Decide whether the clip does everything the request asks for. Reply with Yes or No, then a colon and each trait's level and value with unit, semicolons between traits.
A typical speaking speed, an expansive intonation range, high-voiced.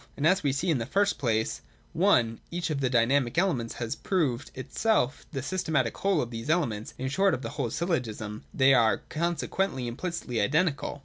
No: average, 190 wpm; wide, 6.4 semitones; low, 135 Hz